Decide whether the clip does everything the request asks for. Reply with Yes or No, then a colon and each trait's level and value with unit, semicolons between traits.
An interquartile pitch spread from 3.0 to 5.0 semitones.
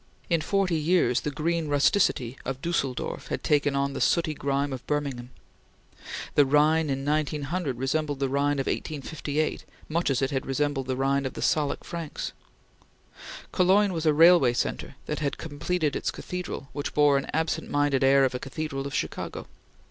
No: narrow, 2.6 semitones